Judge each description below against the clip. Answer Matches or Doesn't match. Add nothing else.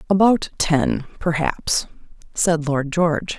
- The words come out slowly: Matches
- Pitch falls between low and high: Matches